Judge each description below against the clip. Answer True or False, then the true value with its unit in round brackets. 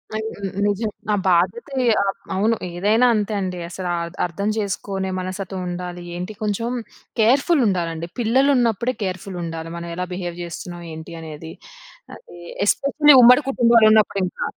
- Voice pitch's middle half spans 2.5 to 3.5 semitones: False (4.5 semitones)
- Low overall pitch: False (195 Hz)